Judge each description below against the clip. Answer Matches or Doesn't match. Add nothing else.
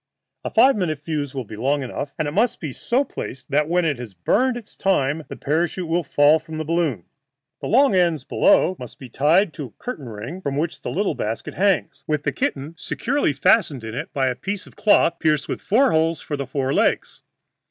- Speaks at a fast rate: Matches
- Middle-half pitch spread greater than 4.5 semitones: Matches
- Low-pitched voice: Doesn't match